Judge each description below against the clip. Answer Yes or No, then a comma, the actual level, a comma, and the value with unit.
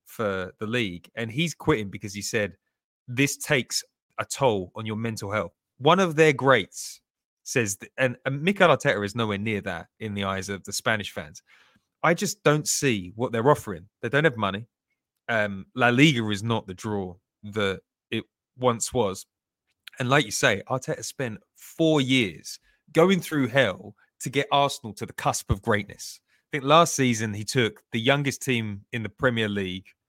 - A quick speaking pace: No, average, 180 wpm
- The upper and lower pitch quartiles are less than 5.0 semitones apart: No, wide, 5.5 semitones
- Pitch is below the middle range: Yes, low, 115 Hz